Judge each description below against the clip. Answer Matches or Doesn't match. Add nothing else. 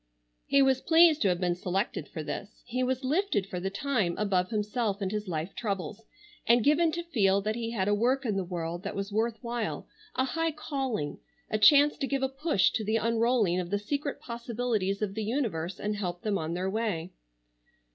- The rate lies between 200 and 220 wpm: Matches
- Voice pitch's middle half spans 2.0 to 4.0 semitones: Doesn't match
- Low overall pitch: Doesn't match